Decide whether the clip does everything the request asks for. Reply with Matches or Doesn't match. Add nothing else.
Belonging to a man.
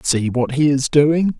Matches